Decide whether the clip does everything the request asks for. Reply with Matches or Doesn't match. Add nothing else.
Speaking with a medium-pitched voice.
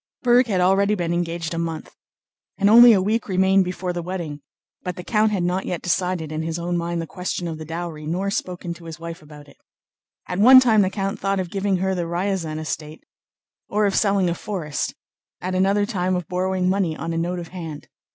Matches